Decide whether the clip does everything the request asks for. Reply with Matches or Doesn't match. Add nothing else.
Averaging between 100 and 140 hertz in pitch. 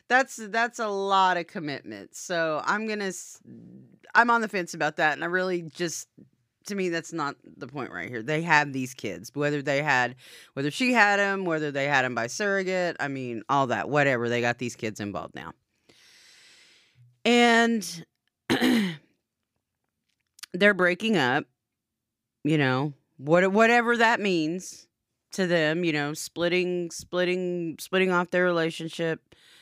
Doesn't match